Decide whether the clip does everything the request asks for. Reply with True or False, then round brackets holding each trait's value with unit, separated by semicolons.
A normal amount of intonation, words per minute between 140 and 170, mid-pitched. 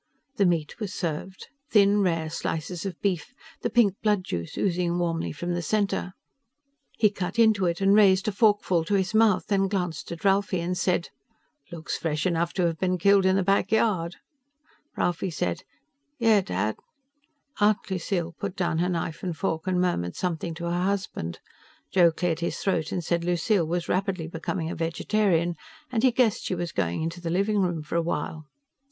False (3.0 semitones; 185 wpm; 180 Hz)